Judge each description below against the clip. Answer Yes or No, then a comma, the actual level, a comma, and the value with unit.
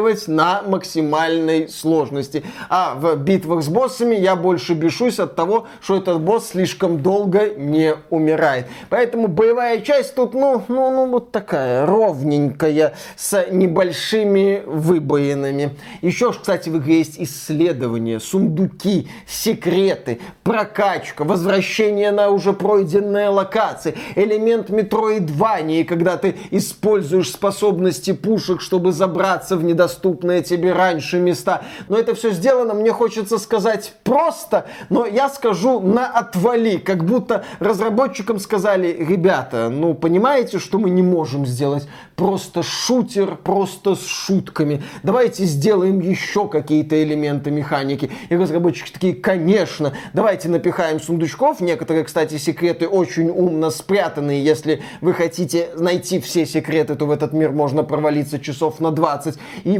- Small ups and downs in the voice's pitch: No, average, 4.4 semitones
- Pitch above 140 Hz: Yes, medium, 185 Hz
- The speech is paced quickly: No, average, 125 wpm